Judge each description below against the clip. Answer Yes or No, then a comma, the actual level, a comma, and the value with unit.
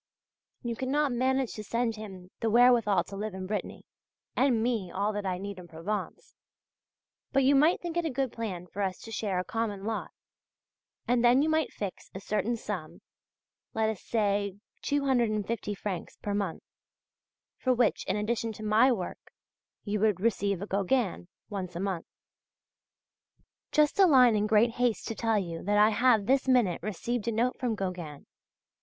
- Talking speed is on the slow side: No, average, 175 wpm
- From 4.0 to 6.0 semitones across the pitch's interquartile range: No, average, 3.6 semitones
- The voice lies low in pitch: No, high, 215 Hz